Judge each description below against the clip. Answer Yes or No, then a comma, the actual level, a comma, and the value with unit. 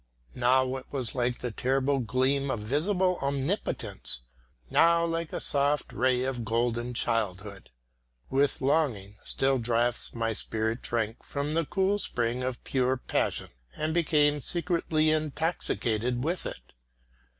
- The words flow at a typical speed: No, slow, 130 wpm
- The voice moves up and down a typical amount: Yes, average, 4.4 semitones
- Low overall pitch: Yes, low, 130 Hz